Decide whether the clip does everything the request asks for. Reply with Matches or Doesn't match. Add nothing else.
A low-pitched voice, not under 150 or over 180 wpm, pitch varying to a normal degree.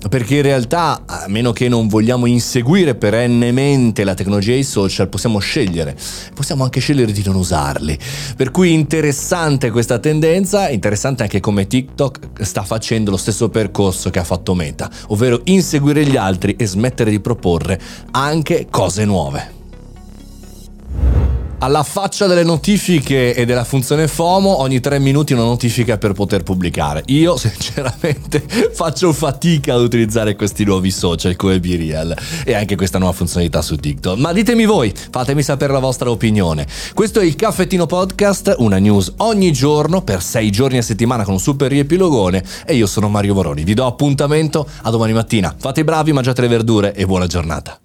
Doesn't match